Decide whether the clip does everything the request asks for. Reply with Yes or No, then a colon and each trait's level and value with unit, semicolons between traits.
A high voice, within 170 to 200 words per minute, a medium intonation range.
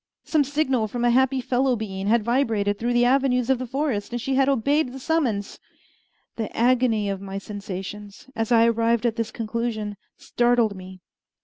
Yes: high, 235 Hz; average, 180 wpm; average, 3.5 semitones